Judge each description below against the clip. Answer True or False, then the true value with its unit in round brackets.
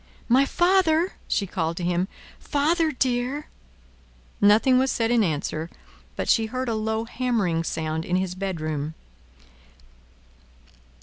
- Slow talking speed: True (125 wpm)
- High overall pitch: True (220 Hz)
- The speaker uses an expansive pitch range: True (7.0 semitones)